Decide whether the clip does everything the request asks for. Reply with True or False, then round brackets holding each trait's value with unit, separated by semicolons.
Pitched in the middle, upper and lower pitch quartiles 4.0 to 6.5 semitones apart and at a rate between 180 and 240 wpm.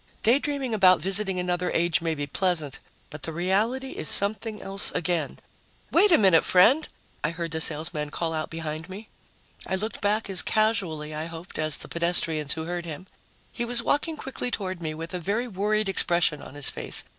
True (180 Hz; 4.7 semitones; 190 wpm)